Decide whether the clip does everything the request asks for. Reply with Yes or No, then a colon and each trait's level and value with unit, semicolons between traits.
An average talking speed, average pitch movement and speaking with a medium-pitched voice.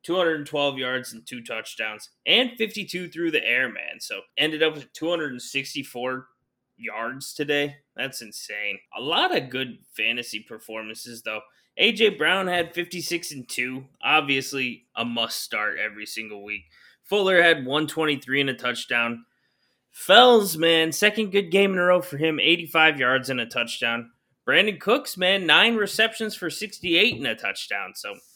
No: average, 150 wpm; wide, 6.2 semitones; medium, 145 Hz